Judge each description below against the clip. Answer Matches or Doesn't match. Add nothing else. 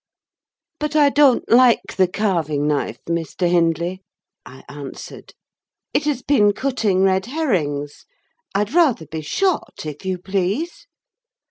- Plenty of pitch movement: Matches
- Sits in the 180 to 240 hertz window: Matches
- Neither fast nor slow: Doesn't match